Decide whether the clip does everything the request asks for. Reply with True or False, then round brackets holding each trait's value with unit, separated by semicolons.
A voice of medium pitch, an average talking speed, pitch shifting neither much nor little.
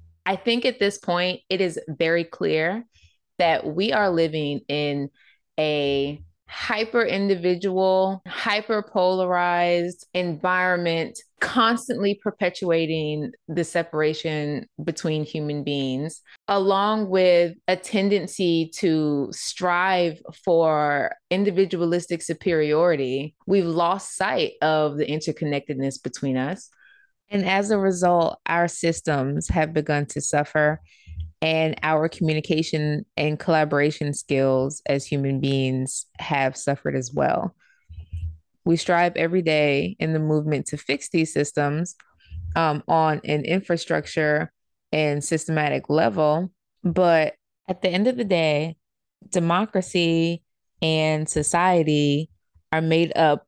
False (160 Hz; 110 wpm; 3.6 semitones)